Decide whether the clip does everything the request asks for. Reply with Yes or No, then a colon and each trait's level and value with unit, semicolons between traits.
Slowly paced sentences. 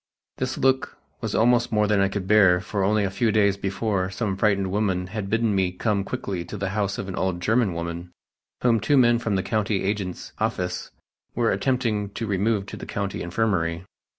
No: average, 200 wpm